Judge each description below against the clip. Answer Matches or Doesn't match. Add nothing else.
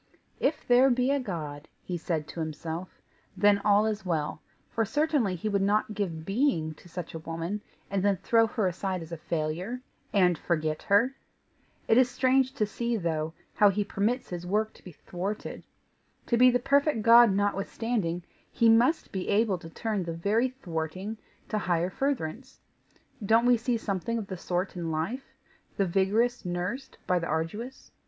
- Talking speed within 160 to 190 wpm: Matches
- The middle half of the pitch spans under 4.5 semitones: Doesn't match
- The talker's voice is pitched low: Doesn't match